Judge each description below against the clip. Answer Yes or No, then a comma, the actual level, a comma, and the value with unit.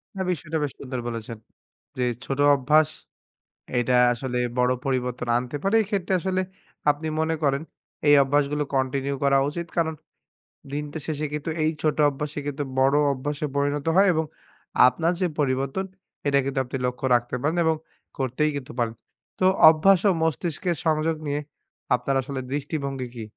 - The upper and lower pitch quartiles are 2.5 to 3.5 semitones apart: Yes, average, 3.2 semitones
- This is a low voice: No, medium, 145 Hz